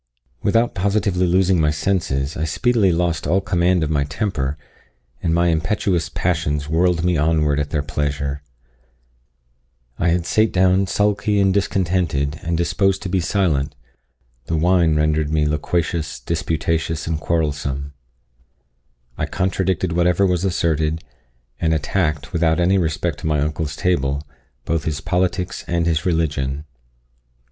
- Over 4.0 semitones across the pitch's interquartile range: No, average, 3.2 semitones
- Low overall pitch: Yes, very low, 85 Hz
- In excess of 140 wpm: No, slow, 135 wpm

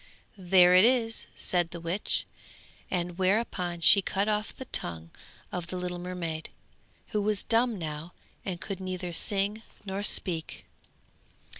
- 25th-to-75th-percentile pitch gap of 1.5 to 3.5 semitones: Yes, average, 2.9 semitones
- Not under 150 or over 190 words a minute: No, average, 140 wpm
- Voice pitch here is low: No, medium, 185 Hz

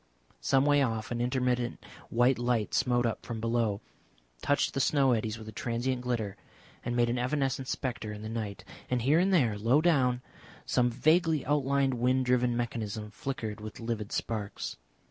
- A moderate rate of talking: Yes, average, 170 wpm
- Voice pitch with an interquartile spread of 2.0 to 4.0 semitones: Yes, average, 2.7 semitones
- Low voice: Yes, low, 120 Hz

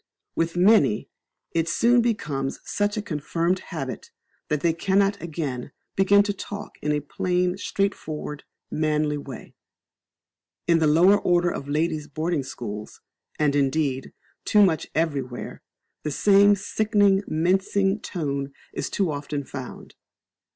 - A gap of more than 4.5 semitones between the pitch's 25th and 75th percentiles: Yes, average, 5.1 semitones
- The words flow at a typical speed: No, slow, 130 wpm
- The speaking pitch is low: No, medium, 165 Hz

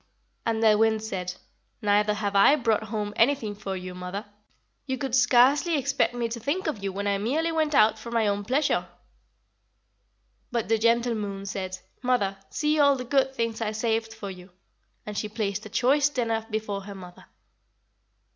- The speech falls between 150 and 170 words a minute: No, average, 180 wpm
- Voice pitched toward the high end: Yes, high, 220 Hz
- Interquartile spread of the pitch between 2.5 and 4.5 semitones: Yes, average, 3.7 semitones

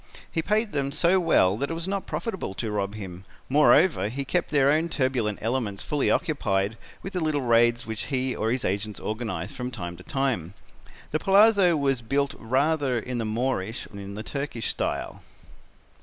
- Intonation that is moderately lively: No, wide, 6.0 semitones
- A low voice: Yes, low, 130 Hz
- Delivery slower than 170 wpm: No, average, 185 wpm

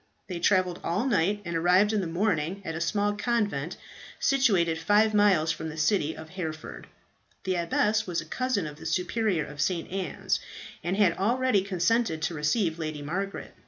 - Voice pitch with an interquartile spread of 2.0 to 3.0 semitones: No, average, 4.1 semitones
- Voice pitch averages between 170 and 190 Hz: Yes, medium, 185 Hz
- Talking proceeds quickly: No, average, 180 wpm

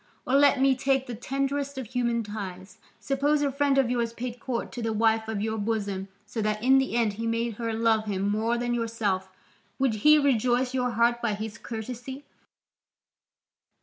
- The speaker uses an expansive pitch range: No, average, 3.2 semitones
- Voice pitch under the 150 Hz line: No, high, 235 Hz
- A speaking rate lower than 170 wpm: No, average, 185 wpm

